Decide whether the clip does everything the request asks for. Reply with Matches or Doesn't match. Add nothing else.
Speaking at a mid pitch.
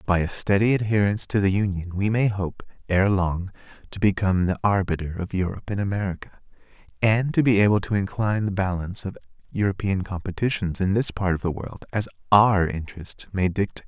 Doesn't match